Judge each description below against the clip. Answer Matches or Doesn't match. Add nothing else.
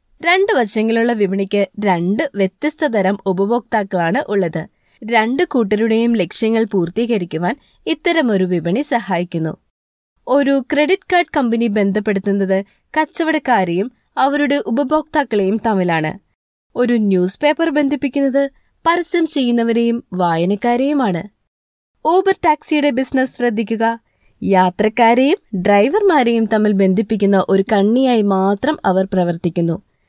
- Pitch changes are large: Matches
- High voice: Matches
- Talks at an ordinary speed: Matches